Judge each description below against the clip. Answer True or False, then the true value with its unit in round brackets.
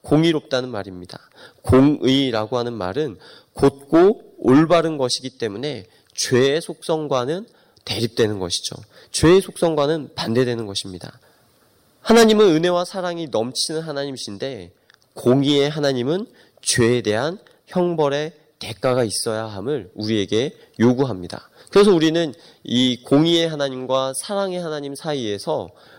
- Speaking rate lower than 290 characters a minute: False (300 characters per minute)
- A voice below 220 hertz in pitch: True (140 Hz)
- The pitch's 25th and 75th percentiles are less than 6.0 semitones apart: True (5.5 semitones)